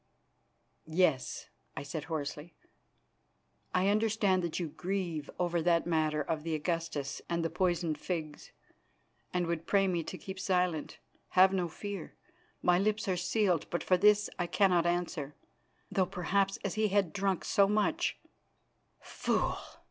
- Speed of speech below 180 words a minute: Yes, average, 150 wpm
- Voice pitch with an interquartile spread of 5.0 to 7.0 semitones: No, average, 3.0 semitones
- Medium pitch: Yes, medium, 180 Hz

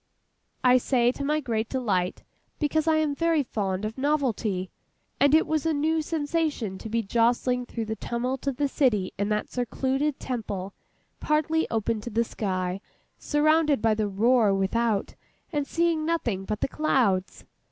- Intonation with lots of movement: Yes, wide, 5.7 semitones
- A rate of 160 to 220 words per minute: Yes, average, 165 wpm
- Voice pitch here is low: No, high, 245 Hz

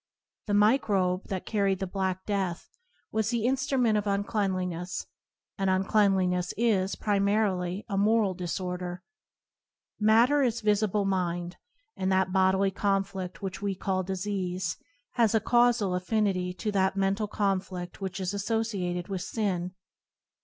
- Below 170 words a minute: Yes, slow, 135 wpm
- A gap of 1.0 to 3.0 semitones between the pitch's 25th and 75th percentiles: Yes, narrow, 2.4 semitones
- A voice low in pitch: No, high, 195 Hz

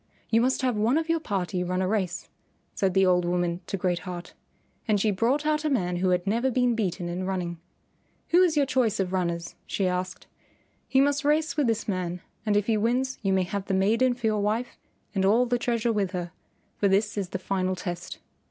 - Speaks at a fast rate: Yes, fast, 220 wpm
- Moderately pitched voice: No, high, 200 Hz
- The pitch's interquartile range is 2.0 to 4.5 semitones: No, average, 4.9 semitones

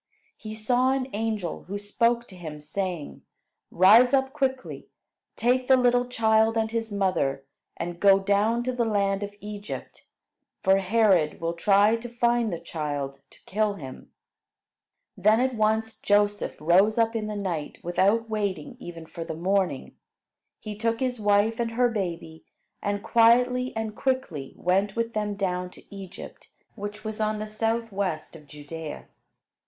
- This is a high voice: Yes, high, 210 Hz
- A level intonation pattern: No, average, 3.8 semitones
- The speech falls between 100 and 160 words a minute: Yes, average, 155 wpm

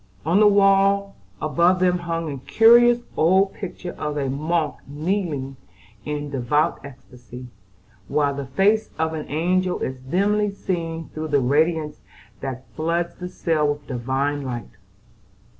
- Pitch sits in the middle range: Yes, medium, 160 Hz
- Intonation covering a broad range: No, average, 4.6 semitones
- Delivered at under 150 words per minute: Yes, average, 140 wpm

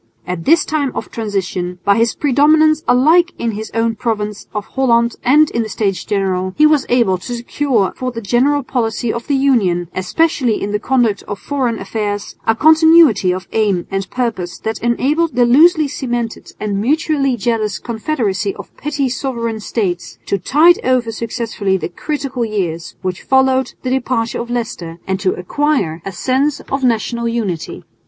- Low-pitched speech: No, high, 235 Hz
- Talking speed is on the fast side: No, average, 170 wpm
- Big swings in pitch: No, average, 4.9 semitones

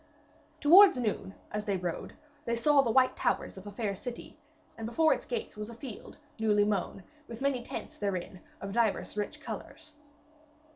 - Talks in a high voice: Yes, high, 225 Hz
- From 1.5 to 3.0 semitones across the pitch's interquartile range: No, average, 4.3 semitones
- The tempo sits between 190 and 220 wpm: No, average, 175 wpm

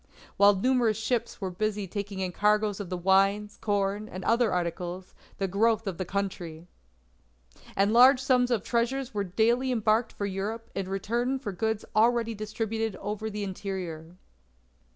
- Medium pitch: No, high, 210 Hz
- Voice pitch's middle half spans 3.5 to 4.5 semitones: No, average, 2.9 semitones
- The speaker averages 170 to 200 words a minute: No, average, 155 wpm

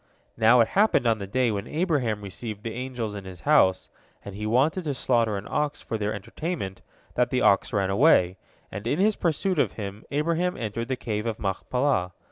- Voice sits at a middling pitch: No, low, 115 Hz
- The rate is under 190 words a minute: No, average, 200 wpm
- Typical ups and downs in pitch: No, wide, 5.9 semitones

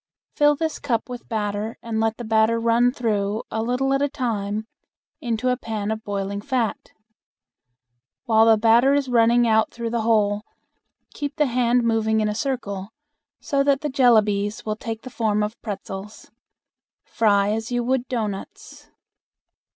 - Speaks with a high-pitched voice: Yes, high, 225 Hz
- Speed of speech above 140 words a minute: Yes, average, 160 wpm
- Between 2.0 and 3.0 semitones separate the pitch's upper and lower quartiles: Yes, narrow, 2.6 semitones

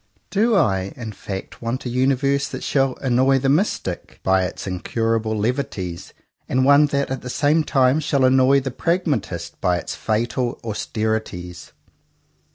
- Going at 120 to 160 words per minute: Yes, average, 150 wpm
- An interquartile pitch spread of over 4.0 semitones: Yes, average, 4.4 semitones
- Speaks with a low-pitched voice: Yes, low, 125 Hz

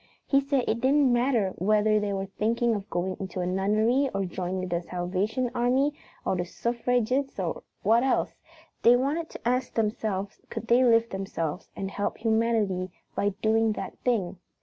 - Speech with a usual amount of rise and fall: Yes, average, 4.1 semitones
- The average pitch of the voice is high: Yes, high, 220 Hz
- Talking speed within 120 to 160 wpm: No, average, 170 wpm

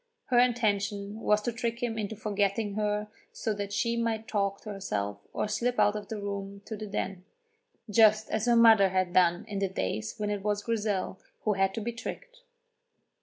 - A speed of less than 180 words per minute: No, average, 195 wpm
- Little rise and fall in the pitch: Yes, narrow, 2.1 semitones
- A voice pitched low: No, high, 210 Hz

